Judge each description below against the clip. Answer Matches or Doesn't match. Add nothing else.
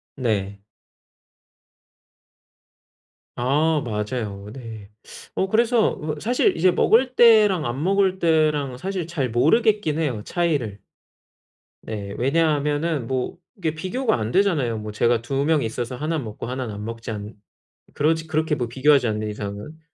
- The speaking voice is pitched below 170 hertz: Matches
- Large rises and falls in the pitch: Matches